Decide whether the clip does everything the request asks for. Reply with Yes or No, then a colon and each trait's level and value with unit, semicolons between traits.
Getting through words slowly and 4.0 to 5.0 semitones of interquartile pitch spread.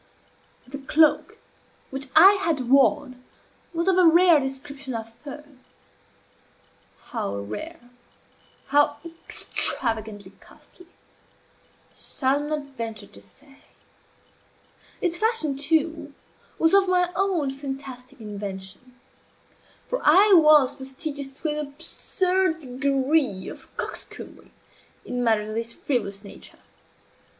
Yes: slow, 105 wpm; average, 4.6 semitones